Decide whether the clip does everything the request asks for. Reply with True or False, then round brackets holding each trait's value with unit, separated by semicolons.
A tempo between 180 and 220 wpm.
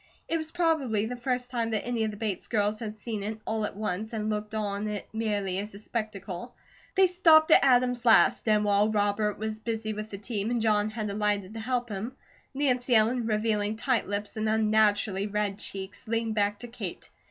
True (205 wpm)